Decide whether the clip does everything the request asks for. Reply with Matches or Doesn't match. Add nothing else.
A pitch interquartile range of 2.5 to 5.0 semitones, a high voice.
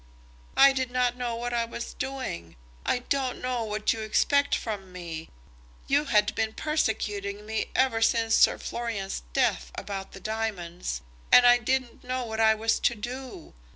Matches